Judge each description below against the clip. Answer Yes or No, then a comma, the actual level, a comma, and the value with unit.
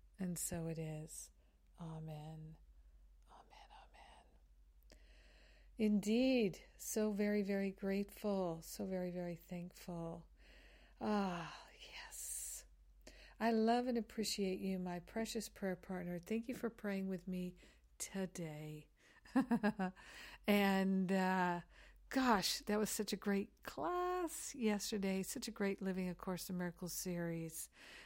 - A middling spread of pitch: Yes, average, 4.0 semitones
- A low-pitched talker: No, high, 190 Hz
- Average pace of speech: No, slow, 115 wpm